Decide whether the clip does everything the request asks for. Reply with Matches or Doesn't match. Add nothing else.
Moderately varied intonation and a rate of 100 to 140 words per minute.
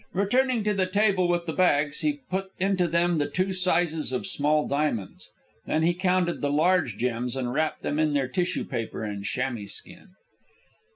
Doesn't match